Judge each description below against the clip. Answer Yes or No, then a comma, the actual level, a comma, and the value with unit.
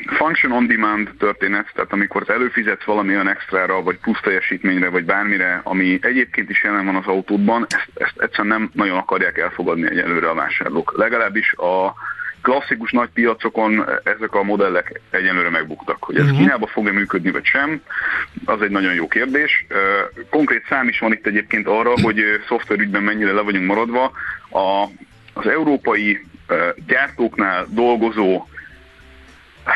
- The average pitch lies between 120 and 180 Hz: No, low, 100 Hz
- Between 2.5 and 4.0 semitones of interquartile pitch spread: Yes, average, 2.8 semitones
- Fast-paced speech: No, average, 145 wpm